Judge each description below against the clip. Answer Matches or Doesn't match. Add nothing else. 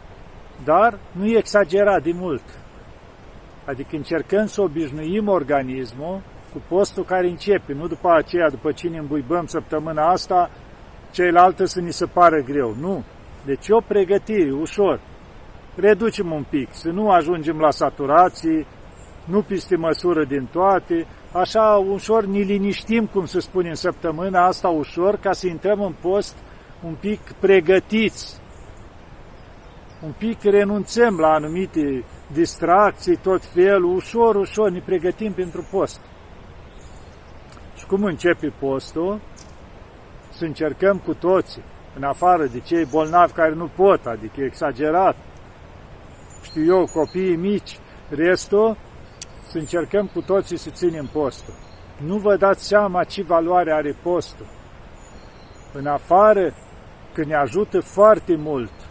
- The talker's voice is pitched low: Doesn't match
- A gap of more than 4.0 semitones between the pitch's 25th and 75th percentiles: Matches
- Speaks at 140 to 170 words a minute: Doesn't match